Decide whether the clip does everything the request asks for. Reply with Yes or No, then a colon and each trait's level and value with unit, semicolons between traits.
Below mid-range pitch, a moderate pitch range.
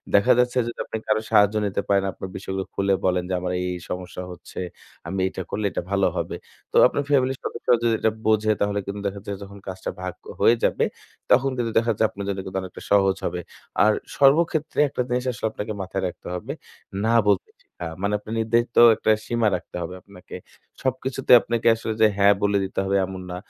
Yes: low, 100 Hz; average, 3.5 semitones